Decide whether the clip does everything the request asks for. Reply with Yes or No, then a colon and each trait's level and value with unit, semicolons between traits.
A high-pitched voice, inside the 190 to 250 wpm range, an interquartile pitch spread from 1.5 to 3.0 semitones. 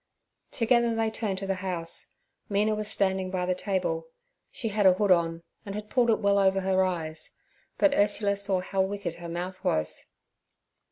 No: high, 195 Hz; average, 180 wpm; narrow, 2.5 semitones